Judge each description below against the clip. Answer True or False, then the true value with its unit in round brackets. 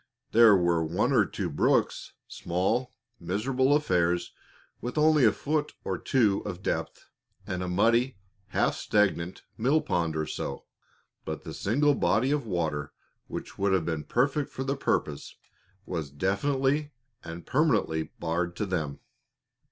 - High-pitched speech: False (100 Hz)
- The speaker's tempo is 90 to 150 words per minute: True (145 wpm)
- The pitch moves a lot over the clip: True (7.6 semitones)